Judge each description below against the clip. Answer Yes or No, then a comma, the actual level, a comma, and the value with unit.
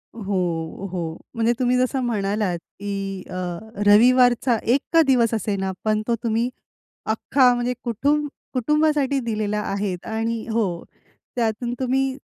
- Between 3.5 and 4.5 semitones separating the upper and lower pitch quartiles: Yes, average, 3.9 semitones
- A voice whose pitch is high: Yes, high, 230 Hz